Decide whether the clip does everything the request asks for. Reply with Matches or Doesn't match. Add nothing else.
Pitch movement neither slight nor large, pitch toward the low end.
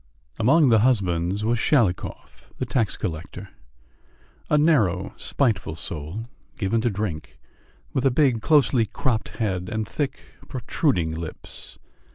Doesn't match